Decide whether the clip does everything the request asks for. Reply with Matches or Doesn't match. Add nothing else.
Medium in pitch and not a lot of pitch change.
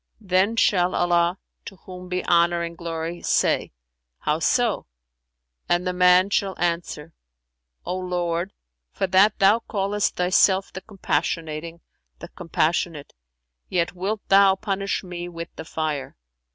Matches